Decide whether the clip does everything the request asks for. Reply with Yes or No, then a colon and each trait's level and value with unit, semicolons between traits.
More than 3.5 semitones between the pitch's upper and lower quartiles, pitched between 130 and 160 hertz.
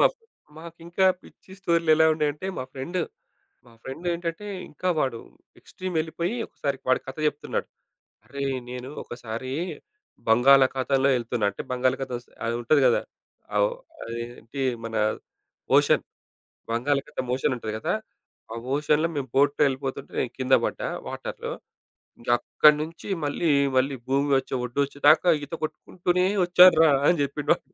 Yes: average, 4.1 semitones; medium, 140 Hz